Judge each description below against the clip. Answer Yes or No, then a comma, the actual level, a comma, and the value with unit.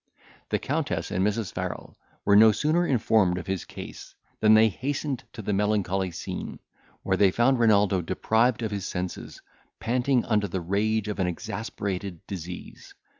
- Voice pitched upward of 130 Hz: No, low, 105 Hz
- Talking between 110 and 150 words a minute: No, average, 160 wpm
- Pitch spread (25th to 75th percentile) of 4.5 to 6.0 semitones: No, average, 3.0 semitones